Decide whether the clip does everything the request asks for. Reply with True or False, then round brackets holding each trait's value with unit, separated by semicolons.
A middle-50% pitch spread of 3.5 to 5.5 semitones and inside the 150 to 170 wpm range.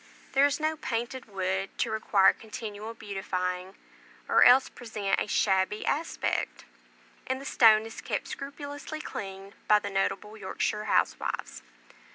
False (4.9 semitones; 135 wpm)